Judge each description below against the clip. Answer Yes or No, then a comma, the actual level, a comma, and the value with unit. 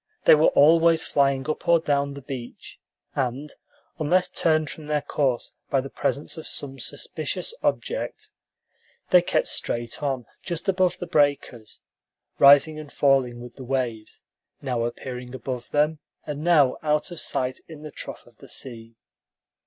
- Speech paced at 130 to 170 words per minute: Yes, average, 155 wpm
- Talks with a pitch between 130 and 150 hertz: Yes, medium, 140 Hz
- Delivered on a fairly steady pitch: No, average, 3.4 semitones